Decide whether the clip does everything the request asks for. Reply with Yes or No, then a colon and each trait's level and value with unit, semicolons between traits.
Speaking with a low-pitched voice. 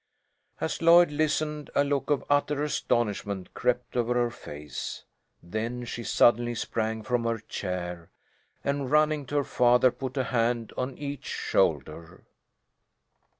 Yes: low, 125 Hz